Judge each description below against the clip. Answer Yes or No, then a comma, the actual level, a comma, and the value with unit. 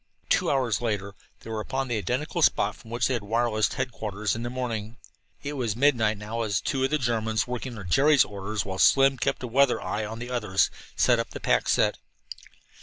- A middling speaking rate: No, fast, 210 wpm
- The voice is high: No, low, 115 Hz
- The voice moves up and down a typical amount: Yes, average, 3.3 semitones